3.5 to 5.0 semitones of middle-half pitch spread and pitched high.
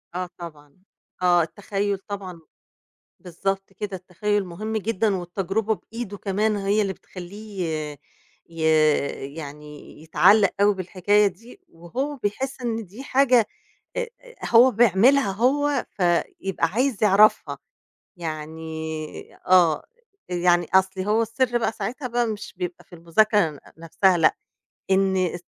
Yes: average, 3.8 semitones; high, 195 Hz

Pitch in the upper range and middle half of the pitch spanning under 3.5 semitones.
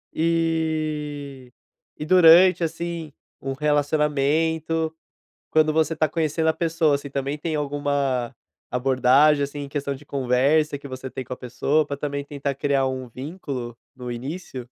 No: medium, 145 Hz; average, 2.7 semitones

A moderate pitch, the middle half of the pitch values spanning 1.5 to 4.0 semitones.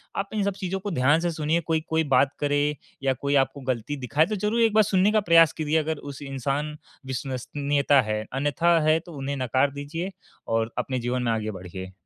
No: medium, 145 Hz; average, 4.4 semitones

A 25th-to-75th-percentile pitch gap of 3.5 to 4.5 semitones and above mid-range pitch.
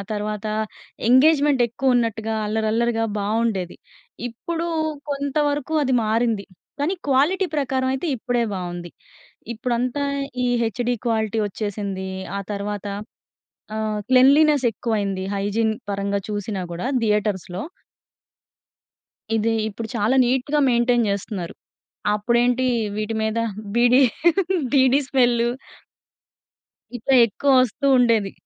Yes: average, 3.8 semitones; high, 230 Hz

